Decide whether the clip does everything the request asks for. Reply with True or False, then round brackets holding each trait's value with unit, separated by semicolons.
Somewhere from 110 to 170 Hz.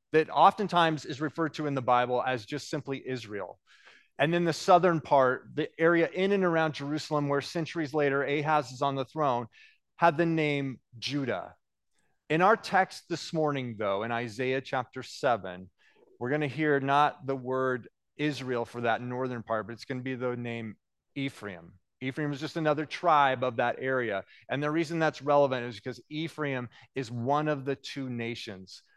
True (140 Hz)